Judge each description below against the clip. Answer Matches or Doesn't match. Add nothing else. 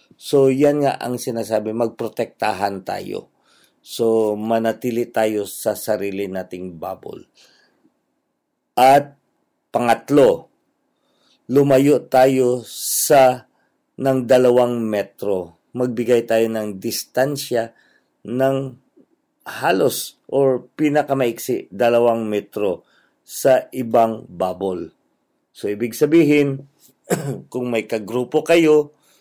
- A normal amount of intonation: Matches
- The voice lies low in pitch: Matches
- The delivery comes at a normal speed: Doesn't match